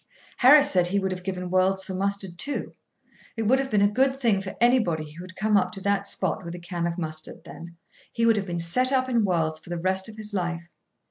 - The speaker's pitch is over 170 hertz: Yes, high, 190 Hz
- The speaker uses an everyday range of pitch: Yes, average, 3.9 semitones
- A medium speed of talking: No, fast, 250 wpm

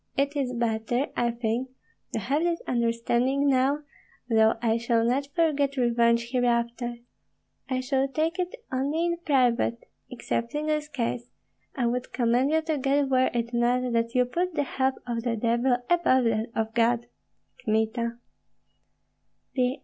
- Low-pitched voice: No, very high, 250 Hz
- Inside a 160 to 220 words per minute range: No, average, 150 wpm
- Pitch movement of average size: Yes, average, 3.0 semitones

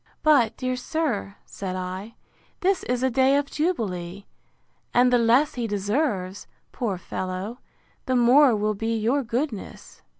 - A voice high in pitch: Yes, high, 235 Hz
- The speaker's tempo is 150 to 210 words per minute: No, average, 140 wpm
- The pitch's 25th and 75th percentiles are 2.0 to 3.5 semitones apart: No, average, 4.7 semitones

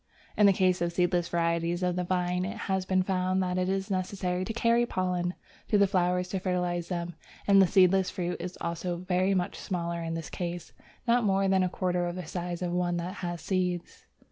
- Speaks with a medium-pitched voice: Yes, medium, 180 Hz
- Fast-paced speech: Yes, fast, 215 wpm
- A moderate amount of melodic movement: No, narrow, 1.4 semitones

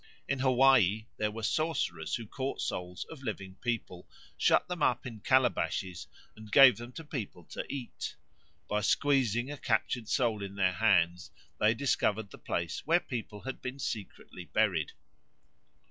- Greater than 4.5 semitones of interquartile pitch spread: Yes, average, 5.1 semitones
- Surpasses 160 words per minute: No, average, 155 wpm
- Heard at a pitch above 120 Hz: No, low, 110 Hz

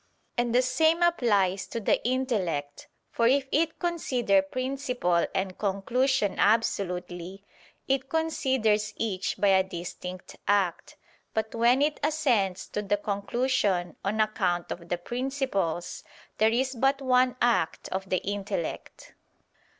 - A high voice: Yes, high, 220 Hz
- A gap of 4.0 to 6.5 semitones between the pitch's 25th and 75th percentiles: Yes, wide, 5.4 semitones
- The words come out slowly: Yes, slow, 125 wpm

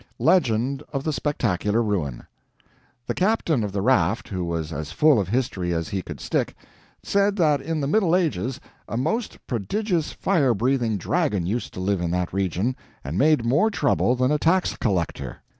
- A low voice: Yes, low, 120 Hz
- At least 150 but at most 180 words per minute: Yes, average, 175 wpm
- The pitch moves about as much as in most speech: No, wide, 8.6 semitones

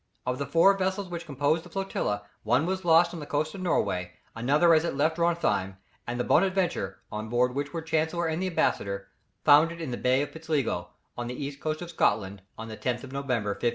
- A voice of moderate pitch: Yes, medium, 145 Hz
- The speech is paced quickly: Yes, fast, 225 wpm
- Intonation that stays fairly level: No, wide, 5.6 semitones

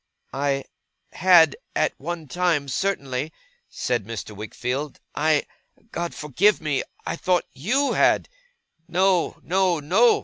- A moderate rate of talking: No, slow, 115 wpm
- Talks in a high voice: No, medium, 155 Hz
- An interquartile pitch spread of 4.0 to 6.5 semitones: Yes, average, 4.8 semitones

